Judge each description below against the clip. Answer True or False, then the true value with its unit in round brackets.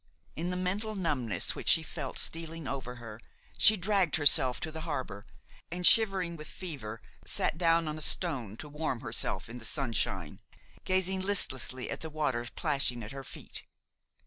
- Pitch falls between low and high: True (155 Hz)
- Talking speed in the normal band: True (170 wpm)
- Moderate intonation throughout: False (6.2 semitones)